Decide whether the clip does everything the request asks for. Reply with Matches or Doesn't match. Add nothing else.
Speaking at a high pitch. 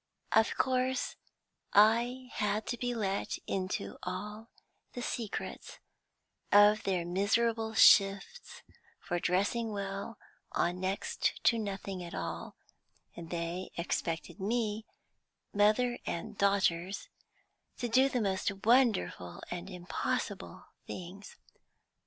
Matches